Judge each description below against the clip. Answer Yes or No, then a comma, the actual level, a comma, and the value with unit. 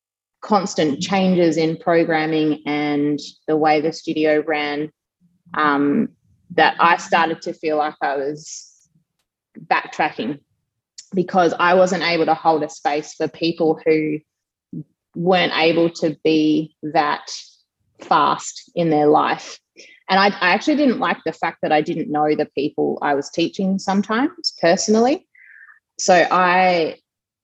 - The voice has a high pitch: No, medium, 160 Hz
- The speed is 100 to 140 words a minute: Yes, slow, 135 wpm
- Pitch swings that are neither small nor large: Yes, average, 3.1 semitones